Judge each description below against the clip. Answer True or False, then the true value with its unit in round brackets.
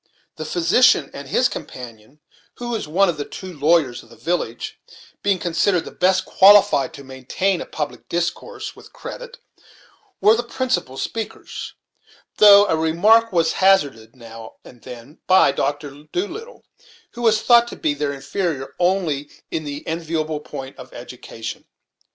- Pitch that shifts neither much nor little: False (6.0 semitones)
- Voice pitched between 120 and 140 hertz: False (165 Hz)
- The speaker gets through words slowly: False (150 wpm)